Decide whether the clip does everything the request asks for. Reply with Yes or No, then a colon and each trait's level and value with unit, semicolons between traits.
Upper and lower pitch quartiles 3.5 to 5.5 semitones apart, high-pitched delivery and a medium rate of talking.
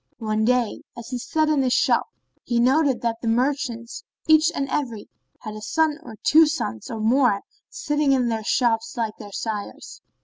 Yes: average, 4.1 semitones; high, 240 Hz; average, 180 wpm